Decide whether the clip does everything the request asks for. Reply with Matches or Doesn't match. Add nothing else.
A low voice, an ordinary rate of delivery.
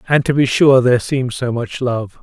Doesn't match